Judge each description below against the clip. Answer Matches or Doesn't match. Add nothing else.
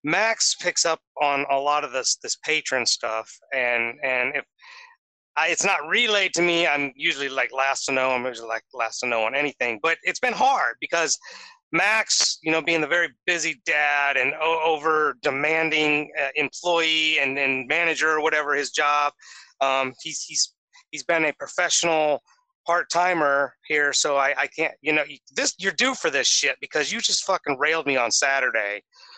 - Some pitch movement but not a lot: Matches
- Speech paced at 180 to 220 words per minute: Matches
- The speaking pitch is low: Doesn't match